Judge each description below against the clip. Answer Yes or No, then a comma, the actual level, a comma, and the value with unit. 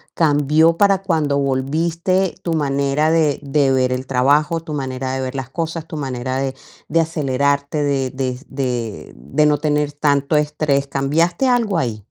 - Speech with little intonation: No, average, 3.2 semitones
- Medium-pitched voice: Yes, medium, 145 Hz